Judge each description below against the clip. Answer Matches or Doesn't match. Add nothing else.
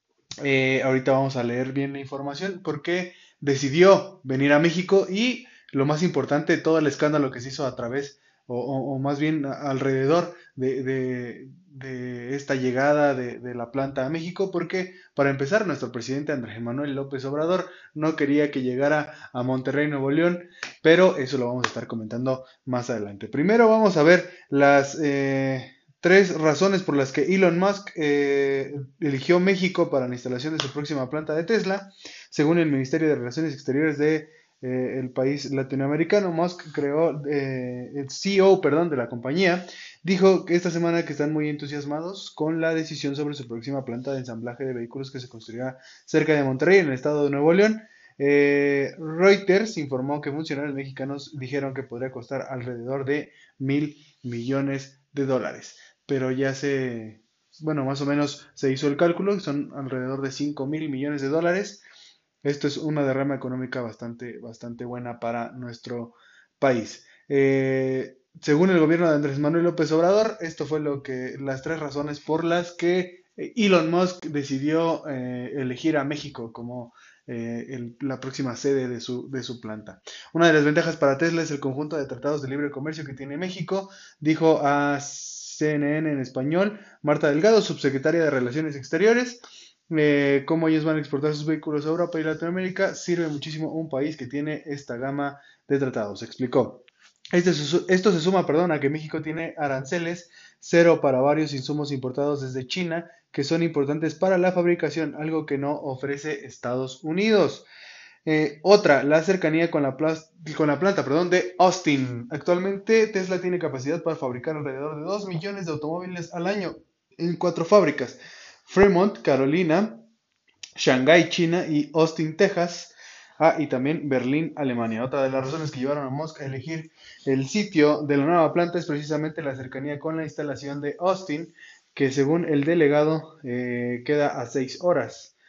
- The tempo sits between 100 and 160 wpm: Doesn't match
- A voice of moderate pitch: Matches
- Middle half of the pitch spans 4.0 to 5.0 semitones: Doesn't match